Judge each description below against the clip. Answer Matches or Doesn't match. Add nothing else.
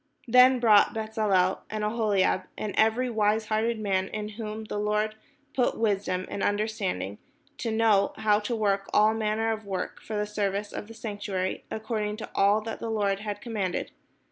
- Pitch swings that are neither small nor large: Doesn't match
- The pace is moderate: Matches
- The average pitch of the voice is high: Matches